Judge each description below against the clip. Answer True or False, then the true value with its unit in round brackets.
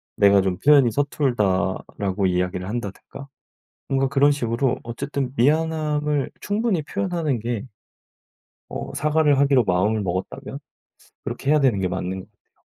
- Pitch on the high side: False (130 Hz)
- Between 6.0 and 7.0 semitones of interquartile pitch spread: True (6.7 semitones)